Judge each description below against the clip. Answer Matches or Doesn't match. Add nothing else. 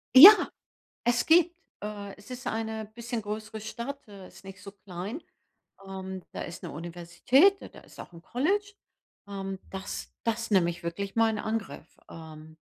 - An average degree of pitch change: Matches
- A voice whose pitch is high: Matches